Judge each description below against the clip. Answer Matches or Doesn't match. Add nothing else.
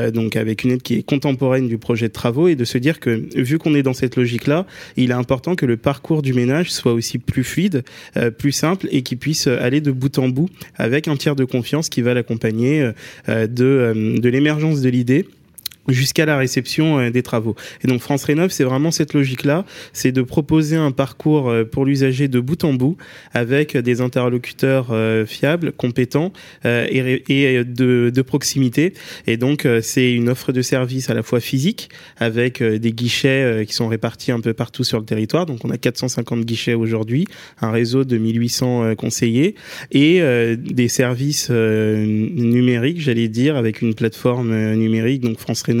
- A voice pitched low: Matches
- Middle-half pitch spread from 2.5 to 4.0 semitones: Matches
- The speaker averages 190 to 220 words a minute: Doesn't match